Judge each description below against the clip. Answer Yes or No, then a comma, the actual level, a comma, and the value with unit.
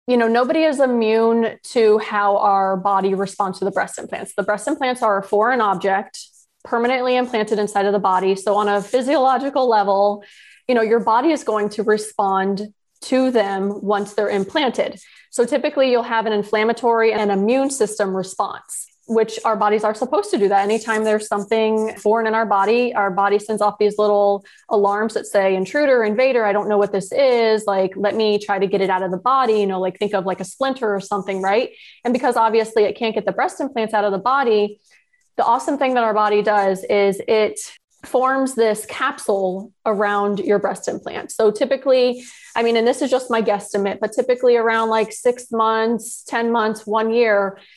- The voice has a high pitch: Yes, high, 215 Hz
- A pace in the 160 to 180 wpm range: No, average, 200 wpm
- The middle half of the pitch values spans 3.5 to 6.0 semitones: No, average, 3.1 semitones